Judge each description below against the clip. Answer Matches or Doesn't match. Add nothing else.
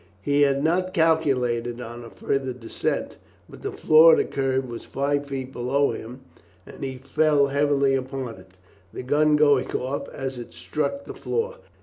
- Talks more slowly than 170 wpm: Doesn't match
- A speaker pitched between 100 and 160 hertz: Matches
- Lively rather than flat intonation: Doesn't match